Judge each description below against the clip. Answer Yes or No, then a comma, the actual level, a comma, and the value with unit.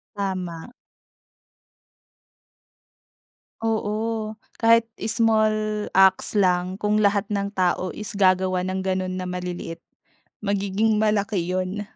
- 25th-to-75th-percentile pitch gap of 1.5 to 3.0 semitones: Yes, narrow, 2.5 semitones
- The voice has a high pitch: Yes, high, 200 Hz